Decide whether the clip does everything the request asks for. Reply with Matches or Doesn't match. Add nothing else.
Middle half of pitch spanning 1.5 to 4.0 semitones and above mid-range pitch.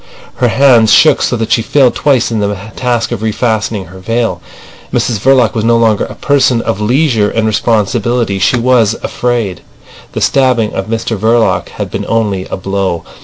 Doesn't match